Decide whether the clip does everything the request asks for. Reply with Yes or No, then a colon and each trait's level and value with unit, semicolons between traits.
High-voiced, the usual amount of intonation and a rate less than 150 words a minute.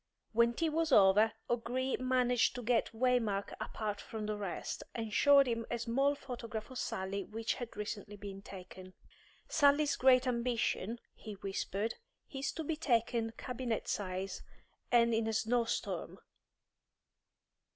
Yes: high, 230 Hz; average, 3.2 semitones; average, 140 wpm